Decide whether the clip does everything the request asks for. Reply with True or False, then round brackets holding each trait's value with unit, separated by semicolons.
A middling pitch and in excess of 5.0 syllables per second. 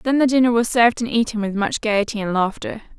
False (225 Hz; 6.2 syllables/s)